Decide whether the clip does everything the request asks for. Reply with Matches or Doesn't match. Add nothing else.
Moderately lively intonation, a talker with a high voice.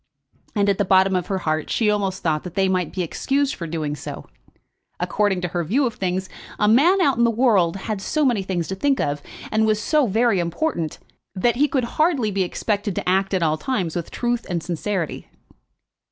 Matches